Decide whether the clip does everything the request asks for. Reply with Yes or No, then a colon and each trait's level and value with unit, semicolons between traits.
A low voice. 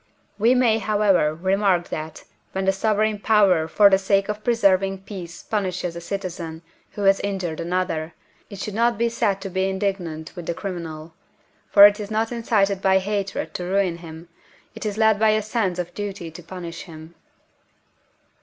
No: high, 195 Hz